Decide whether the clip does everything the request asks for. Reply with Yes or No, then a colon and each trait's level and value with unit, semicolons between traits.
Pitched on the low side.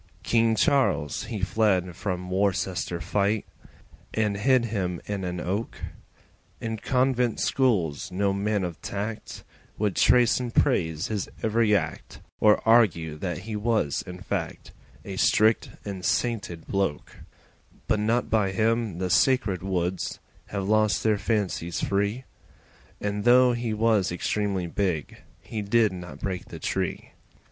Yes: low, 100 Hz